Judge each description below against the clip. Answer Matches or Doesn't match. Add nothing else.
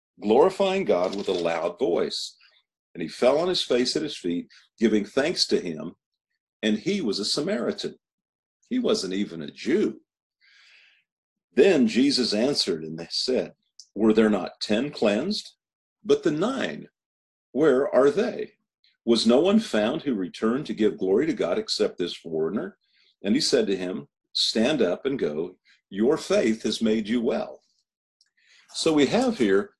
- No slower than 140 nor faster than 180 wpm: Matches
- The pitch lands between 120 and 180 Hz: Doesn't match